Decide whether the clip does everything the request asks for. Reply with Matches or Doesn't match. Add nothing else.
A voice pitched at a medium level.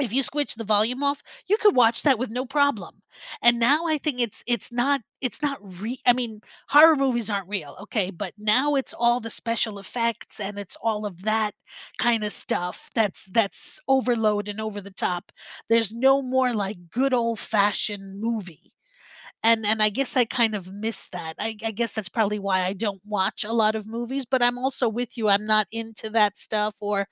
Doesn't match